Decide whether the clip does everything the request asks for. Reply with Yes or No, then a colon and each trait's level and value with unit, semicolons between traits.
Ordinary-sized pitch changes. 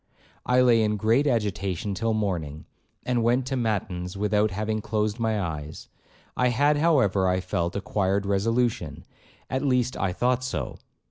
Yes: average, 4.2 semitones